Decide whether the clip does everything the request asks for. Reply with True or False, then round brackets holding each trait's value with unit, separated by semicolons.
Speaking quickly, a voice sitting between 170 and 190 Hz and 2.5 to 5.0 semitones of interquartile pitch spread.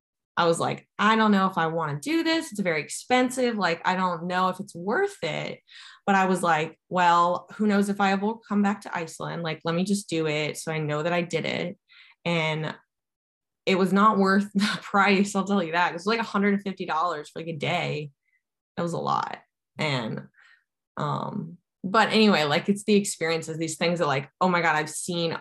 True (215 wpm; 185 Hz; 3.5 semitones)